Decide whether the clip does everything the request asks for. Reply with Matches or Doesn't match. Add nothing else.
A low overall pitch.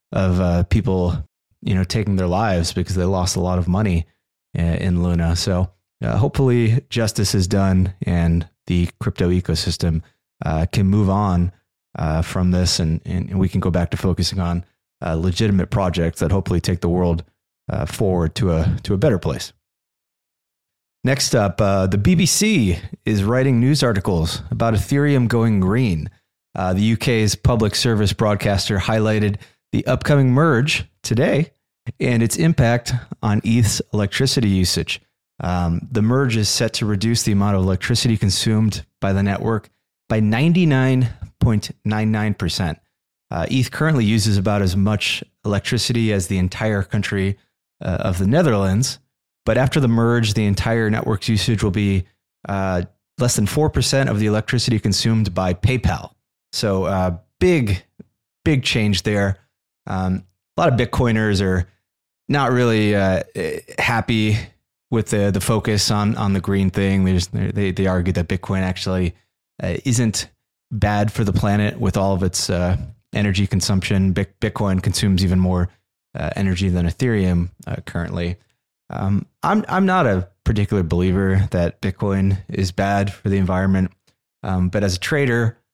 Matches